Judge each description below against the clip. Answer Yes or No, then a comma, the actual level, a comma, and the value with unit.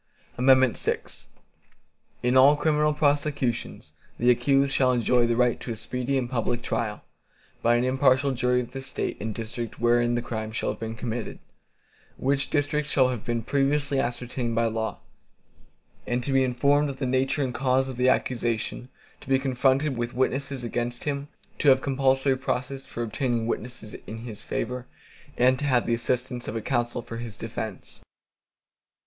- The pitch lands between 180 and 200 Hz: No, low, 125 Hz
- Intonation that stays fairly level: Yes, narrow, 2.2 semitones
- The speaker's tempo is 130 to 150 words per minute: No, average, 170 wpm